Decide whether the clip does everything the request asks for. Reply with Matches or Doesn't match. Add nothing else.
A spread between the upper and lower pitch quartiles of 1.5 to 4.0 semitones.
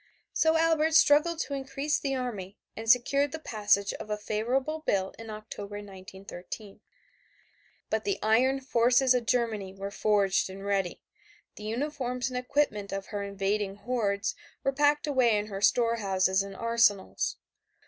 Doesn't match